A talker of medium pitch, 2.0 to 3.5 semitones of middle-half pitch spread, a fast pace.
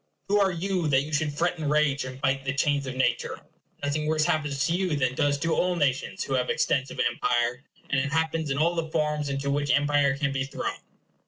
Yes: medium, 145 Hz; narrow, 2.5 semitones; fast, 225 wpm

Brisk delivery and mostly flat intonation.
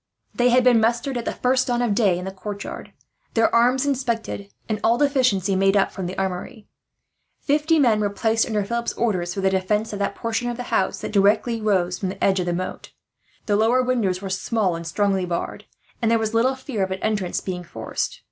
No: fast, 220 wpm; average, 3.9 semitones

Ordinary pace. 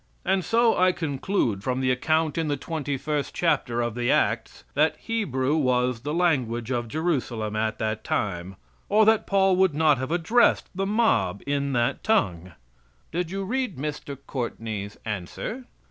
Yes: average, 160 wpm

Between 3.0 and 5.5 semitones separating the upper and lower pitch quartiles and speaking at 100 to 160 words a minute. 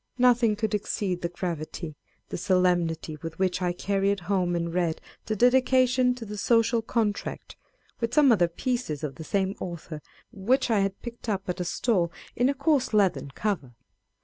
No: average, 5.2 semitones; average, 175 wpm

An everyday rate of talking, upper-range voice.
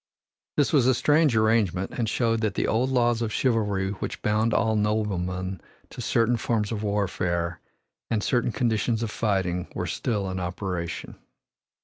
No: average, 155 wpm; low, 110 Hz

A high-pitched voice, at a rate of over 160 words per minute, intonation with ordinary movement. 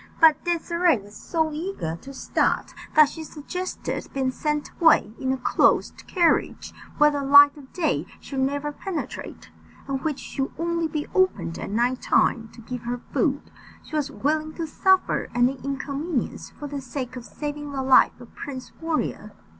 Yes: very high, 285 Hz; average, 170 wpm; average, 3.4 semitones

